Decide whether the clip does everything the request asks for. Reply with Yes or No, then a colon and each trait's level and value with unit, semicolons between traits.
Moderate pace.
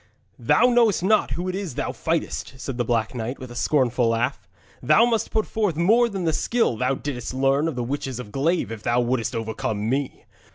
No: fast, 210 wpm